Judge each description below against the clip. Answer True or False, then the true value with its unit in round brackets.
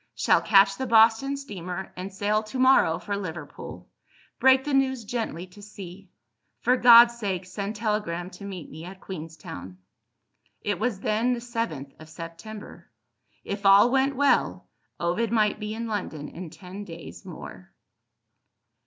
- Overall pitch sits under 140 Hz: False (205 Hz)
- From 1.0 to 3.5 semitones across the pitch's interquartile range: False (4.4 semitones)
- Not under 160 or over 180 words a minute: False (150 wpm)